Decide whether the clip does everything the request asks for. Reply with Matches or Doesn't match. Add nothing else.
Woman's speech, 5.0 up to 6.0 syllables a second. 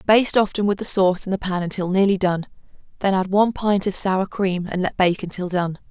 Matches